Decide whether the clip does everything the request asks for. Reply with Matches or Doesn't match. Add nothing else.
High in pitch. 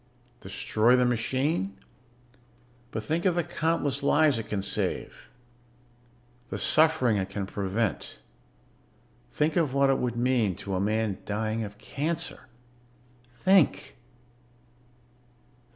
Doesn't match